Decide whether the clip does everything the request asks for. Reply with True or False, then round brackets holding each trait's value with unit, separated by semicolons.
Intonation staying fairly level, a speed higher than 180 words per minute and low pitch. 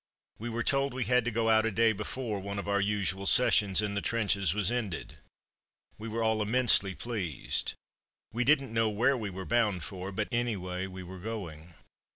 False (3.2 semitones; 195 wpm; 105 Hz)